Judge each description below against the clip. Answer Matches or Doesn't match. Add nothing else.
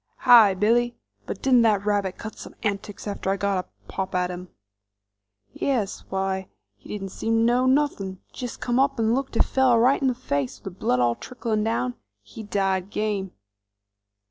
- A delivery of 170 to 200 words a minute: Matches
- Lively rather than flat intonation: Doesn't match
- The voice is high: Matches